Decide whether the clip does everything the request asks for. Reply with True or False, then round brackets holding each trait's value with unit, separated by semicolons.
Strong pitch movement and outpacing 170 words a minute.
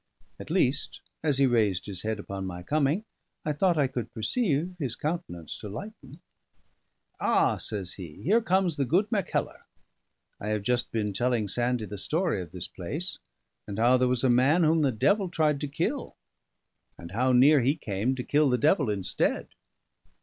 True (6.7 semitones; 180 wpm)